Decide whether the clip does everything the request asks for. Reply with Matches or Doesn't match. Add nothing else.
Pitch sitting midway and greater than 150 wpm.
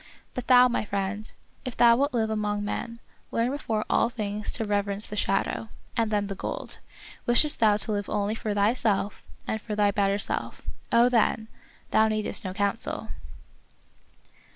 Doesn't match